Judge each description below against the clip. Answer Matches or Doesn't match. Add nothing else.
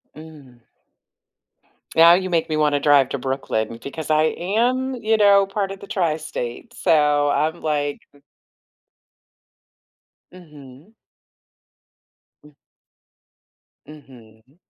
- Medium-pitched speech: Matches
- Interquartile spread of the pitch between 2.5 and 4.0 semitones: Doesn't match